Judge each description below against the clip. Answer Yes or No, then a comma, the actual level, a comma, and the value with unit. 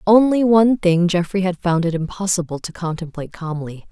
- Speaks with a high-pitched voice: No, medium, 180 Hz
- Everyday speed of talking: Yes, average, 170 wpm